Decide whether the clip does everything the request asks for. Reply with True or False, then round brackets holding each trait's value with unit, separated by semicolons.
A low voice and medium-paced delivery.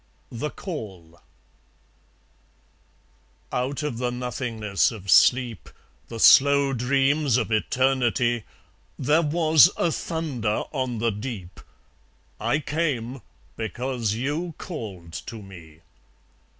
False (125 Hz; 100 wpm)